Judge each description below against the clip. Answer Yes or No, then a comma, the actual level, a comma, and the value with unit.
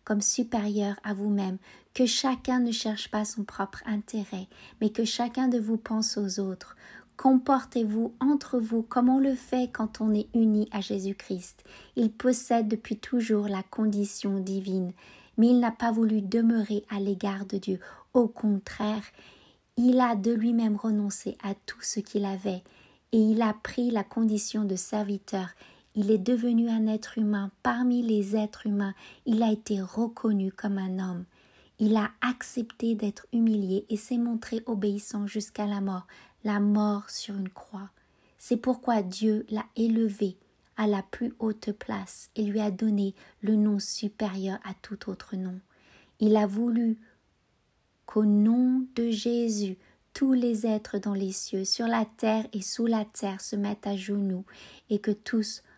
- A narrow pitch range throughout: Yes, narrow, 2.3 semitones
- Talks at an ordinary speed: Yes, average, 170 wpm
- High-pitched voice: Yes, high, 215 Hz